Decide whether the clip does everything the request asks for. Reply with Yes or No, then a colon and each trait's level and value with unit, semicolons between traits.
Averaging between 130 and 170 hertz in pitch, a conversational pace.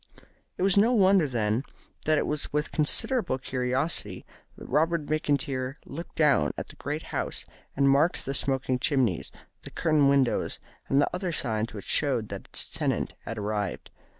Yes: medium, 140 Hz; average, 165 wpm